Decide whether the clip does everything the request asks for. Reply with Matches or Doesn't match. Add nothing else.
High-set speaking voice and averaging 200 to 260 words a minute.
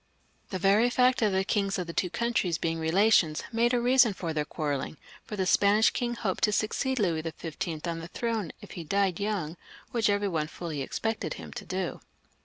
Matches